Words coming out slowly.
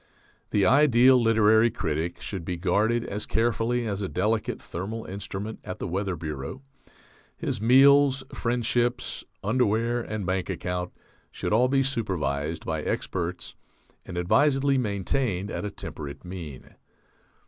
Yes: slow, 130 wpm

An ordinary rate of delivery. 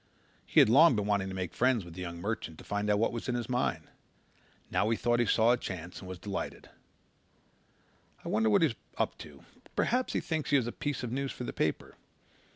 No: fast, 230 wpm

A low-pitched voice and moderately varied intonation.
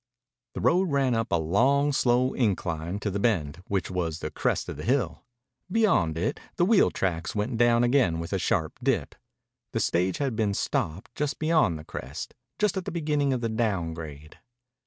No: low, 110 Hz; wide, 8.5 semitones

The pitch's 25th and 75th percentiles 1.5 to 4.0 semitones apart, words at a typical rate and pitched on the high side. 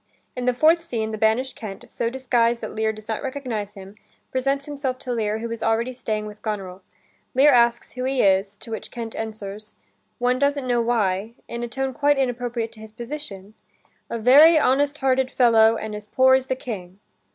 Yes: average, 3.3 semitones; average, 195 wpm; high, 235 Hz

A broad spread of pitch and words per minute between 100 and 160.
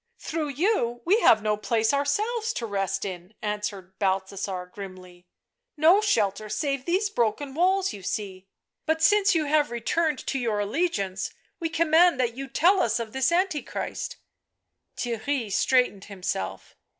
Yes: wide, 8.5 semitones; average, 155 wpm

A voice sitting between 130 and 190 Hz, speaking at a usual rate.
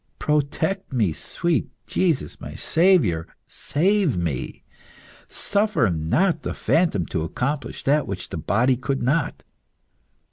No: medium, 140 Hz; slow, 115 wpm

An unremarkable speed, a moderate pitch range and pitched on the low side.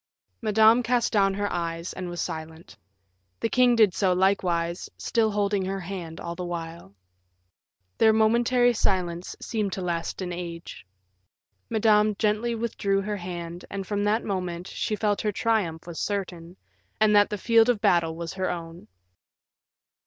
No: average, 155 wpm; average, 3.8 semitones; high, 195 Hz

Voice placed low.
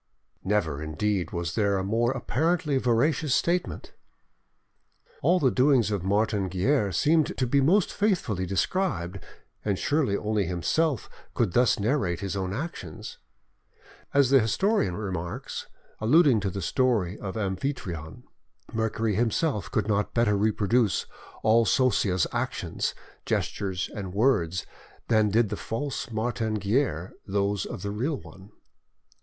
Yes: low, 110 Hz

